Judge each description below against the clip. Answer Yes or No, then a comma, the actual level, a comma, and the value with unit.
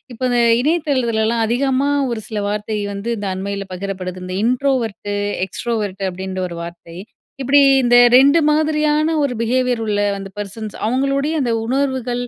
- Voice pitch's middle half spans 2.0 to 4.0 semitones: No, average, 5.1 semitones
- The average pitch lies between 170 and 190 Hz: No, high, 235 Hz